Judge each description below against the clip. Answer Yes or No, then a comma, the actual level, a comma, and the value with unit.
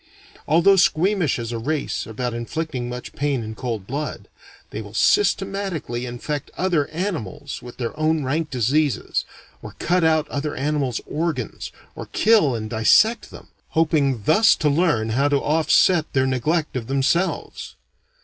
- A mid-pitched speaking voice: Yes, medium, 145 Hz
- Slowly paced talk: No, average, 150 wpm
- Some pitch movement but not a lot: Yes, average, 4.9 semitones